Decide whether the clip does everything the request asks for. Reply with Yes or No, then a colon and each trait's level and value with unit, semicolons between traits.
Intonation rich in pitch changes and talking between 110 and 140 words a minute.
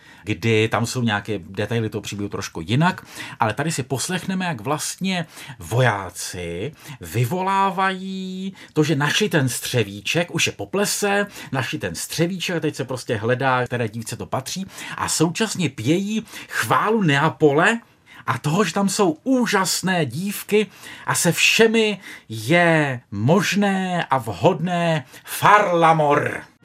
Yes: wide, 7.5 semitones; average, 130 wpm